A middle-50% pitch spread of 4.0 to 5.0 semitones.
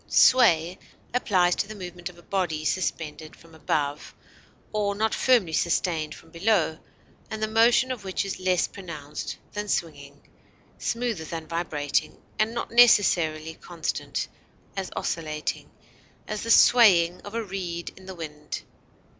Yes: average, 4.7 semitones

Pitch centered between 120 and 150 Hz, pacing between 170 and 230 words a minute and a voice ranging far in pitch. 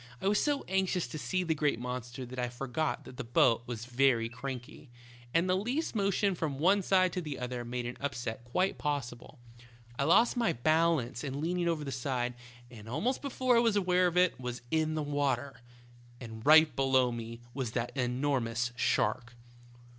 Yes: low, 135 Hz; average, 185 wpm; wide, 6.2 semitones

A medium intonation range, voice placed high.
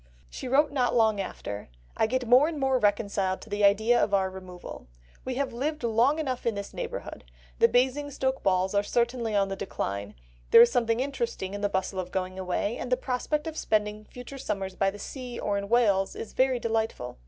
Yes: average, 4.4 semitones; high, 225 Hz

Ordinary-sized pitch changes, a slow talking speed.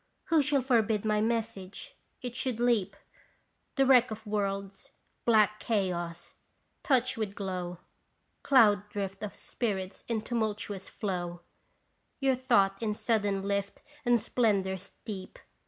Yes: average, 3.3 semitones; slow, 125 wpm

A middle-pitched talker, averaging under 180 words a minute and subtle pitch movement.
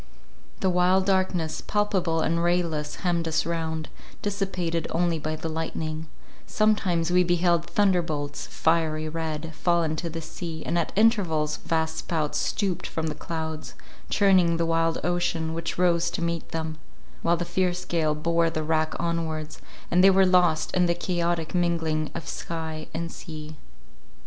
Yes: medium, 165 Hz; average, 155 wpm; narrow, 1.8 semitones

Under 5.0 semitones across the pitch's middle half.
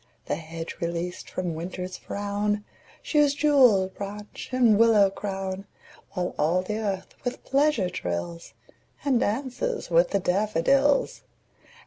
No: average, 5.3 semitones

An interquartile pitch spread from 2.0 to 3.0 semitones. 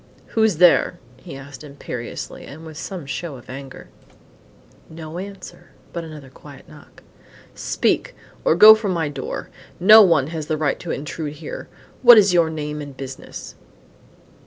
No: average, 3.9 semitones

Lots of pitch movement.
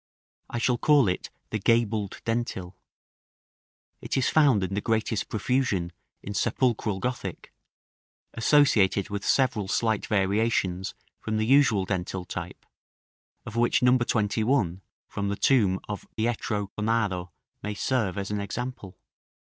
No: average, 3.4 semitones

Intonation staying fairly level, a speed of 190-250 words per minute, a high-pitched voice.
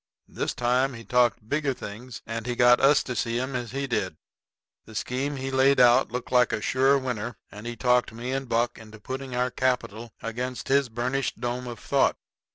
No: narrow, 2.0 semitones; average, 200 wpm; low, 125 Hz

